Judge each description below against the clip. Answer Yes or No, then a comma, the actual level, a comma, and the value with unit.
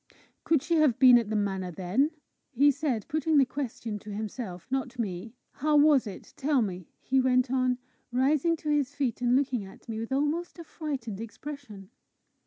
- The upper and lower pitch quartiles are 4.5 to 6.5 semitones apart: Yes, average, 4.9 semitones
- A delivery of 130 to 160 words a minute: No, average, 185 wpm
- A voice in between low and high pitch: No, very high, 255 Hz